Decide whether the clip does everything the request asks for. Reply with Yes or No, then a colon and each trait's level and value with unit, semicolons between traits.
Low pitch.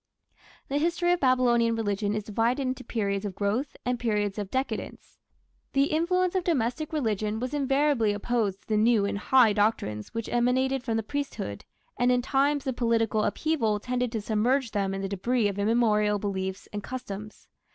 No: high, 230 Hz